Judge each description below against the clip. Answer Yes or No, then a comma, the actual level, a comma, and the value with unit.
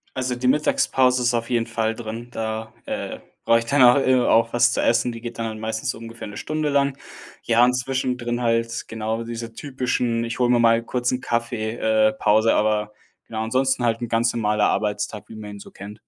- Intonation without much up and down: Yes, narrow, 1.8 semitones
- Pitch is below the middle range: Yes, low, 115 Hz